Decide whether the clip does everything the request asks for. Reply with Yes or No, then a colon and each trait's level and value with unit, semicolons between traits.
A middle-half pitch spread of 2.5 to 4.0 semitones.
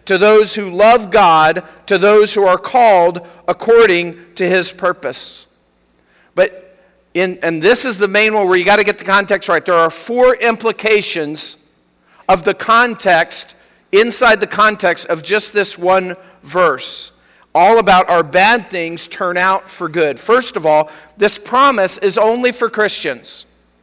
Yes: average, 3.6 semitones